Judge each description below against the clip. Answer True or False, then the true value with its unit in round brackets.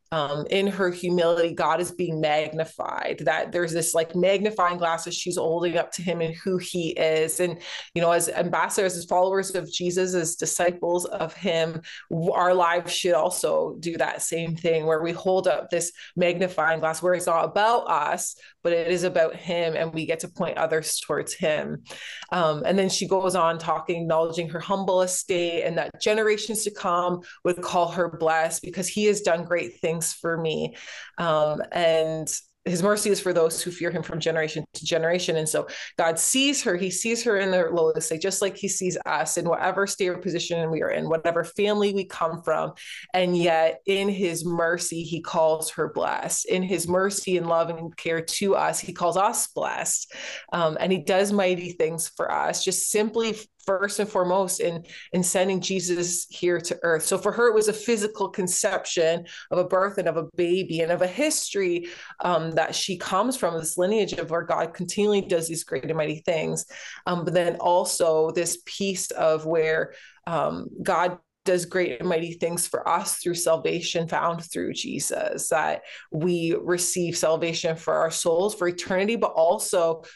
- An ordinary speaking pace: True (190 wpm)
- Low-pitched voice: False (175 Hz)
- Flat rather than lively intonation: True (2.2 semitones)